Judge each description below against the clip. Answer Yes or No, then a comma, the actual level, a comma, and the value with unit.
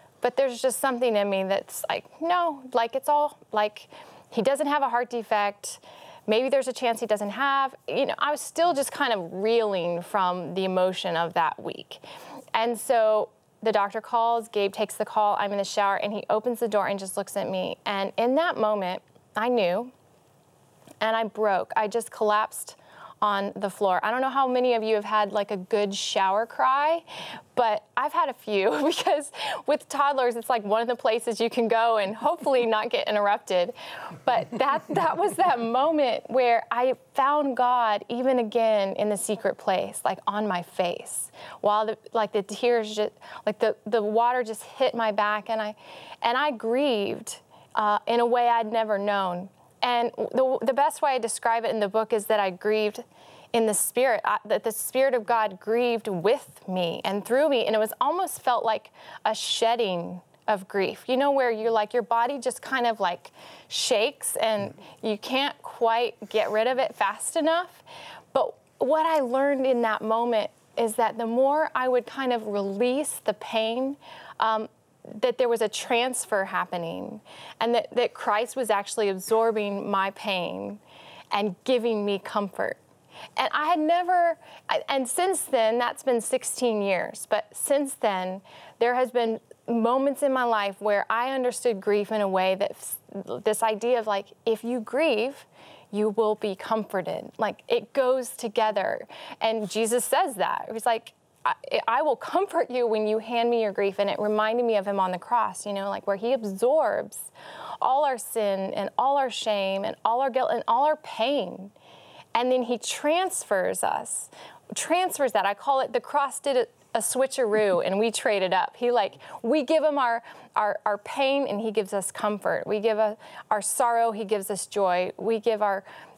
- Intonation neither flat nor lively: Yes, average, 3.9 semitones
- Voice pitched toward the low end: No, high, 230 Hz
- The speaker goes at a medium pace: Yes, average, 190 wpm